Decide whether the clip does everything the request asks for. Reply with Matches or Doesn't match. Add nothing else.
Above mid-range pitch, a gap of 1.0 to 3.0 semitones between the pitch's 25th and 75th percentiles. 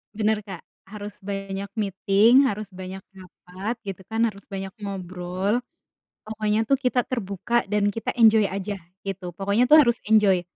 Matches